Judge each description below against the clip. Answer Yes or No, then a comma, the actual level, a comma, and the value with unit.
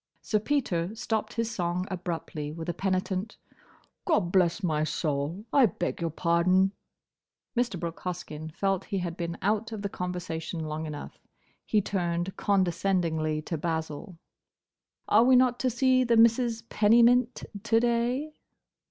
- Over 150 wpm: No, slow, 135 wpm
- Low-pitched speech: No, medium, 185 Hz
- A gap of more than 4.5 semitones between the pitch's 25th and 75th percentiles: Yes, average, 5.1 semitones